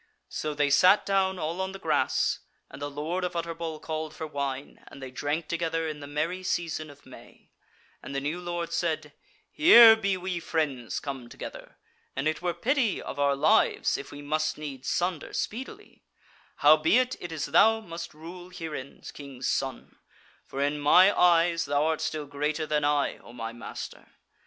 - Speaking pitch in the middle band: Yes, medium, 155 Hz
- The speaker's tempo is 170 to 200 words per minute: Yes, average, 175 wpm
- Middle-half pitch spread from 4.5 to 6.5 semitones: No, average, 3.5 semitones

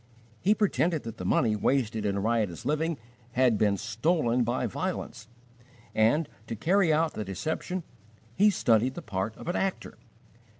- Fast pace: No, average, 155 wpm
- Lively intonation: Yes, wide, 6.8 semitones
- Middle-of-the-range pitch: No, low, 120 Hz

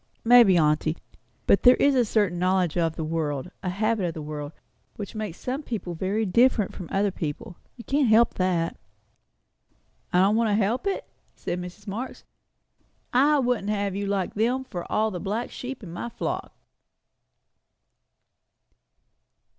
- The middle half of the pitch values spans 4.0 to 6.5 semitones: Yes, average, 4.8 semitones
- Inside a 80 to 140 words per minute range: No, average, 160 wpm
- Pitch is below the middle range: No, high, 200 Hz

